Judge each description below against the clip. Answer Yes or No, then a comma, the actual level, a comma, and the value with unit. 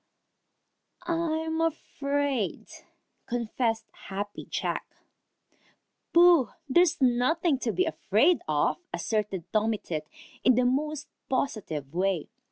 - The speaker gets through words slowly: Yes, slow, 100 wpm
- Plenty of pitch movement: Yes, wide, 7.1 semitones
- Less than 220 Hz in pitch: No, very high, 250 Hz